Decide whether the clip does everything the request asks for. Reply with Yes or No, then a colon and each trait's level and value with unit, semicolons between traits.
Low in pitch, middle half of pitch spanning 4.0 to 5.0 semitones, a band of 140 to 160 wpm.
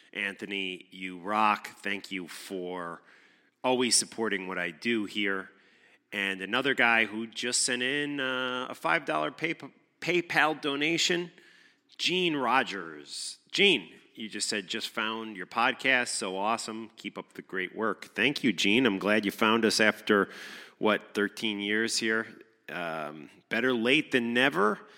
Yes: low, 110 Hz; average, 4.4 semitones; average, 145 wpm